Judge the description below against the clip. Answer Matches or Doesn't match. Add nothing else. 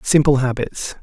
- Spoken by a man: Matches